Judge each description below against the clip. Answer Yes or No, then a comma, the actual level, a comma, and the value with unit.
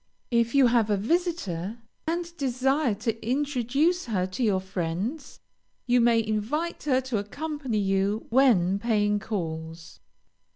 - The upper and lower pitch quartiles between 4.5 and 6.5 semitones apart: Yes, average, 5.3 semitones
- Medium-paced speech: No, slow, 130 wpm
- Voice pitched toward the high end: Yes, high, 230 Hz